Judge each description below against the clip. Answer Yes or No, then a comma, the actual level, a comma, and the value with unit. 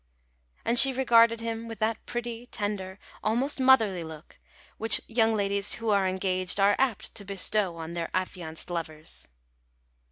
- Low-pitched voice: No, high, 205 Hz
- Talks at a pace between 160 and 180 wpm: No, average, 150 wpm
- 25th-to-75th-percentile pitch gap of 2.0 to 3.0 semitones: No, average, 3.7 semitones